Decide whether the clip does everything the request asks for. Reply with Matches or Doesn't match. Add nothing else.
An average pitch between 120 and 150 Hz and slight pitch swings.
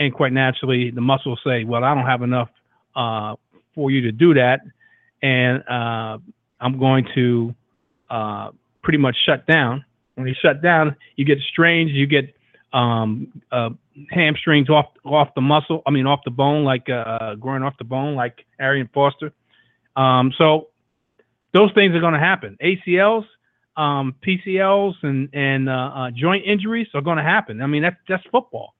Doesn't match